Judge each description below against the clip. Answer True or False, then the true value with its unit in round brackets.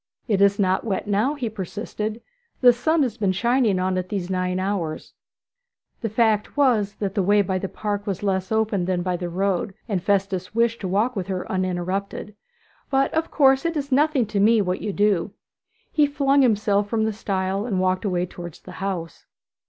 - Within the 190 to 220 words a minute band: True (195 wpm)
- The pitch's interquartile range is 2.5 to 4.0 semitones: True (3.4 semitones)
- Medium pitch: False (200 Hz)